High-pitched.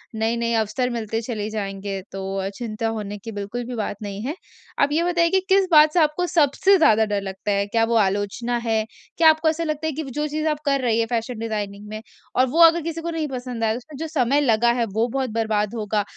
Yes: high, 235 Hz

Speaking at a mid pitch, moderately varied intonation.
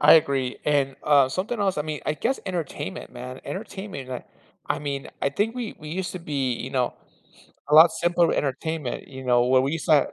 Yes: medium, 150 Hz; average, 4.7 semitones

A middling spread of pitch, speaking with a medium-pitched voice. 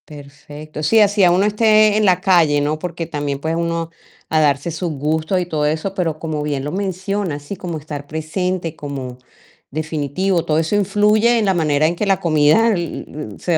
Yes: average, 4.2 semitones; medium, 165 Hz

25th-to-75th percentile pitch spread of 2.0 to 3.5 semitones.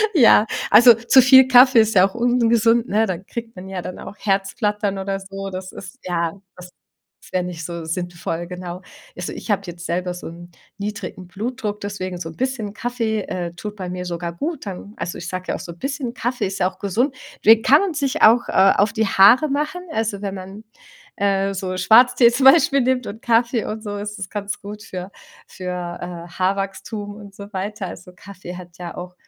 No: average, 4.0 semitones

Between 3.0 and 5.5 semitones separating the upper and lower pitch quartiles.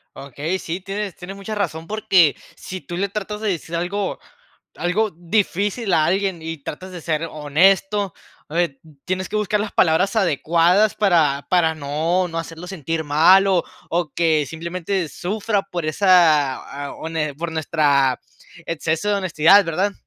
Yes: average, 3.5 semitones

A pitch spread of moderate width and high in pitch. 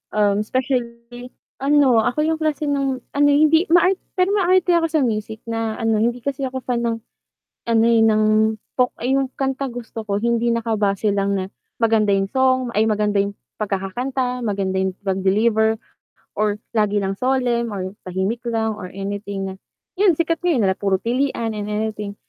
Yes: average, 4.0 semitones; high, 230 Hz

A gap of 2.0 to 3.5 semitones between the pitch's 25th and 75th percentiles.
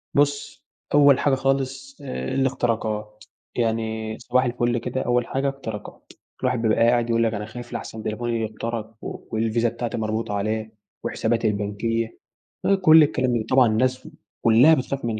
Yes: average, 2.7 semitones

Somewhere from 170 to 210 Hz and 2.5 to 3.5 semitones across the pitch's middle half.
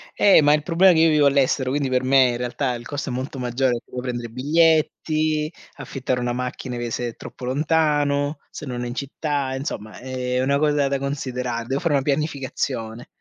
No: low, 135 Hz; average, 2.9 semitones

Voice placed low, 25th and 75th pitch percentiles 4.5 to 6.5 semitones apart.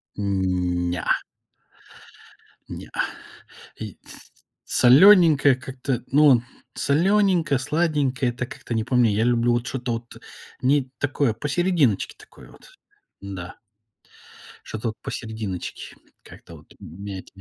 Yes: low, 125 Hz; average, 5.0 semitones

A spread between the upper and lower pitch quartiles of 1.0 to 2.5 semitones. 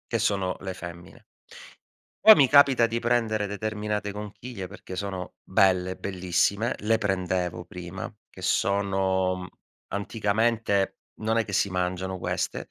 No: average, 2.9 semitones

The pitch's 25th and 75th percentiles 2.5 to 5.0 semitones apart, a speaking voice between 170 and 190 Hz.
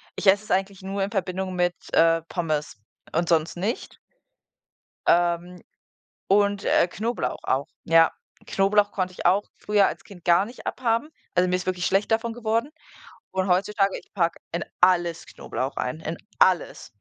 Yes: average, 2.9 semitones; medium, 185 Hz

